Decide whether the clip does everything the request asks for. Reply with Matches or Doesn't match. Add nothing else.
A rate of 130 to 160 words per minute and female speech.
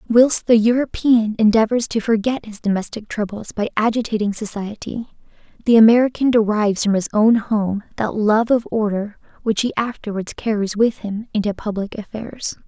Matches